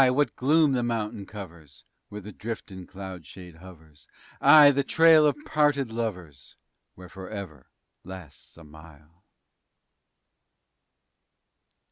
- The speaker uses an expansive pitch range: Yes, wide, 7.3 semitones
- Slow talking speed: Yes, slow, 110 wpm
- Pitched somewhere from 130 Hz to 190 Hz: No, very low, 95 Hz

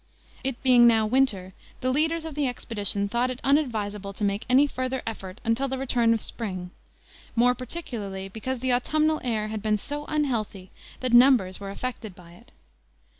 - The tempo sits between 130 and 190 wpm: Yes, average, 175 wpm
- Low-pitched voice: No, high, 240 Hz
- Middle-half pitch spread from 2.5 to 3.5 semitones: No, average, 4.3 semitones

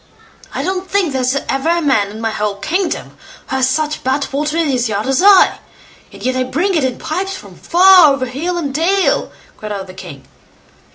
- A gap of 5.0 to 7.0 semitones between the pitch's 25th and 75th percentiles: Yes, wide, 5.4 semitones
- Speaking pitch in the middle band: No, very high, 280 Hz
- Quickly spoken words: Yes, fast, 210 wpm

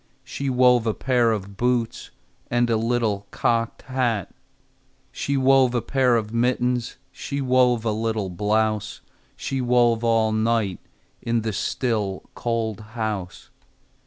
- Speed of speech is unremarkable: No, slow, 130 wpm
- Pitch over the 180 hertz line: No, low, 115 Hz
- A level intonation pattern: Yes, narrow, 2.3 semitones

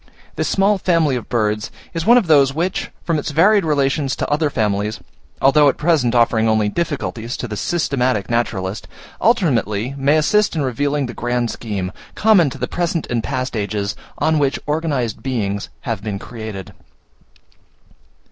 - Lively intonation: Yes, wide, 6.1 semitones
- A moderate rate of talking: Yes, average, 160 wpm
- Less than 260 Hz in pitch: Yes, low, 135 Hz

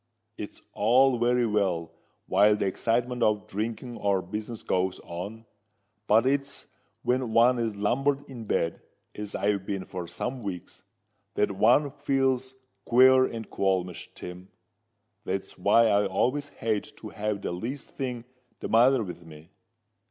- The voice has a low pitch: Yes, low, 110 Hz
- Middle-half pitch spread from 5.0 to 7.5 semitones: No, average, 4.3 semitones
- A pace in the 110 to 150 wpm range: Yes, average, 145 wpm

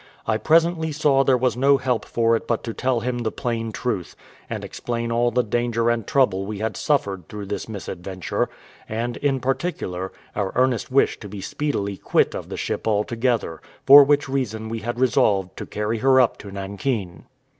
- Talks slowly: No, average, 190 wpm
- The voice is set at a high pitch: No, low, 115 Hz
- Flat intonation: No, average, 4.0 semitones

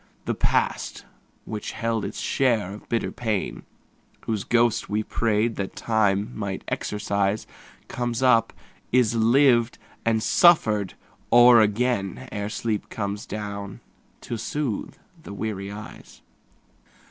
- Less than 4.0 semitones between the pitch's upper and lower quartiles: Yes, narrow, 2.5 semitones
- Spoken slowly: Yes, slow, 120 wpm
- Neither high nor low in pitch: No, low, 110 Hz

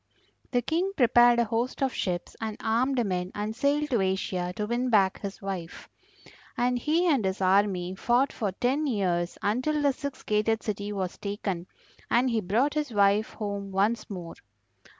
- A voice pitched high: Yes, high, 215 Hz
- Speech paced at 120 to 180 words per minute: Yes, average, 170 wpm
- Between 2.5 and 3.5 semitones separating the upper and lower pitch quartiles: No, average, 4.4 semitones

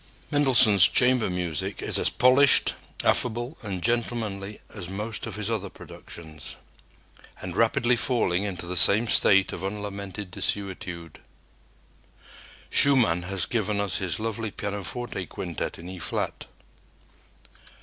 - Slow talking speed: Yes, slow, 120 wpm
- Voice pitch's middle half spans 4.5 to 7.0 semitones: No, average, 4.0 semitones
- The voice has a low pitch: Yes, low, 100 Hz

